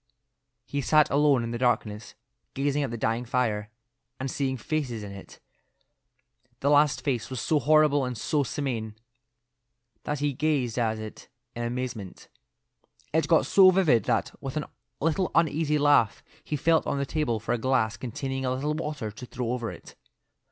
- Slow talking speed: No, average, 170 wpm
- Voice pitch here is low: Yes, low, 130 Hz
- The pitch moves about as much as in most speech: Yes, average, 4.0 semitones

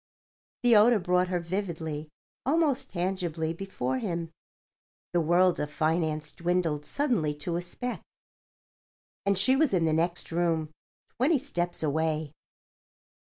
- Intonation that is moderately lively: Yes, average, 3.5 semitones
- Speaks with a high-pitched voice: No, medium, 175 Hz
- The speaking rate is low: Yes, slow, 120 wpm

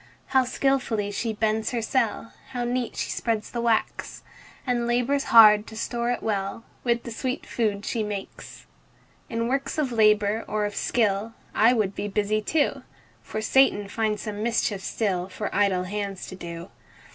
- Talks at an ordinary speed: Yes, average, 170 wpm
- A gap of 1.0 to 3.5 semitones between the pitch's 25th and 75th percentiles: Yes, narrow, 2.6 semitones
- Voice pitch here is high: Yes, high, 220 Hz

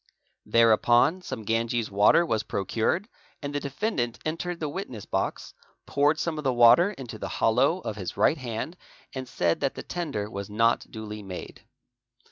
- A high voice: No, low, 120 Hz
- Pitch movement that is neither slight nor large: No, wide, 6.0 semitones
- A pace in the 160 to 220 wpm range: Yes, average, 165 wpm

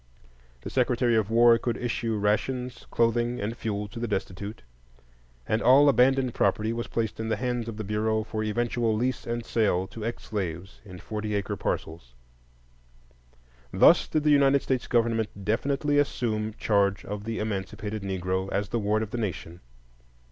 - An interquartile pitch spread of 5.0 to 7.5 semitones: No, narrow, 2.6 semitones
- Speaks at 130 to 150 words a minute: No, average, 165 wpm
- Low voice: Yes, low, 110 Hz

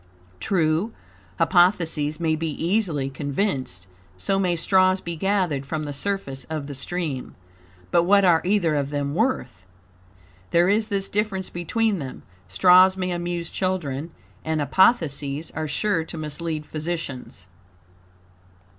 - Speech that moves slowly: Yes, slow, 130 wpm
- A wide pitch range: No, average, 4.4 semitones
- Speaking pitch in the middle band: Yes, medium, 165 Hz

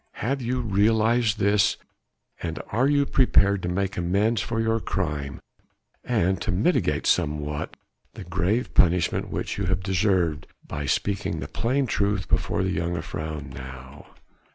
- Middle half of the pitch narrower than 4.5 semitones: No, average, 4.8 semitones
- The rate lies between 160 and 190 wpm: No, average, 140 wpm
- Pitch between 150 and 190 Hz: No, very low, 95 Hz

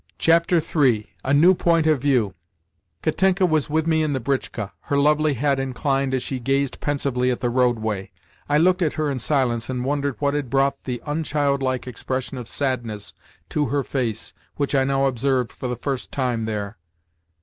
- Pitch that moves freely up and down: No, average, 2.9 semitones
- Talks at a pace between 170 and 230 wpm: Yes, average, 180 wpm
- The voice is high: No, low, 135 Hz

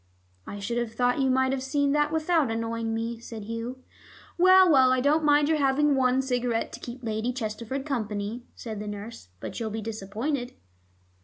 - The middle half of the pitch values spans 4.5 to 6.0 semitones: No, average, 3.5 semitones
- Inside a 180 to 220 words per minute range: Yes, average, 185 wpm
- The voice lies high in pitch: Yes, high, 245 Hz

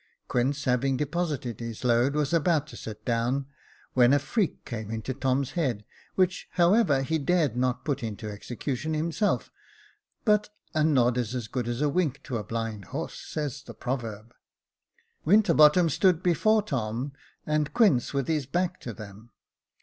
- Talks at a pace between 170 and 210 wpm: No, average, 160 wpm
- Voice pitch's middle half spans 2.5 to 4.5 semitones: No, average, 5.0 semitones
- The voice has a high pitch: No, low, 135 Hz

